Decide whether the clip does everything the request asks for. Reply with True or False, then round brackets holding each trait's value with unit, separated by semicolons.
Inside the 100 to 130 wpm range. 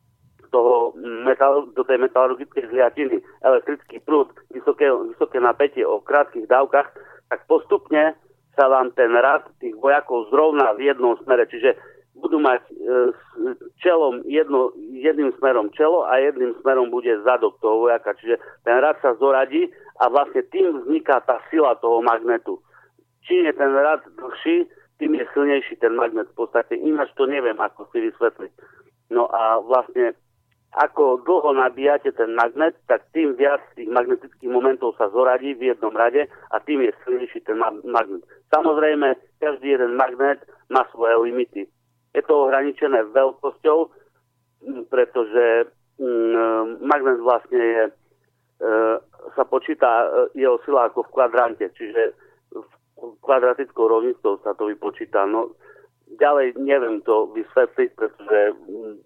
False (140 wpm)